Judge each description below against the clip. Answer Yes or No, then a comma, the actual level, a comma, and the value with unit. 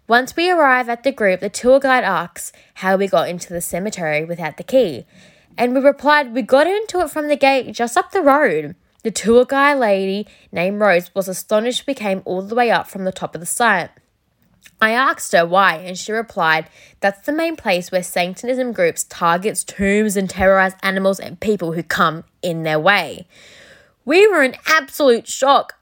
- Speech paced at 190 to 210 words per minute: Yes, average, 195 wpm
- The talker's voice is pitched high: Yes, high, 215 Hz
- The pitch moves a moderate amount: No, wide, 6.5 semitones